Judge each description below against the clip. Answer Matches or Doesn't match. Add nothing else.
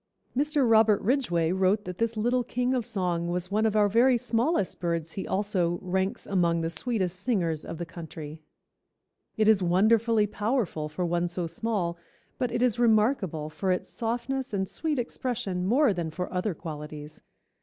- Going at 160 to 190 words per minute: Matches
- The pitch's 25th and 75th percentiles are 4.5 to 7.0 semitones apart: Matches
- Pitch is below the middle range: Doesn't match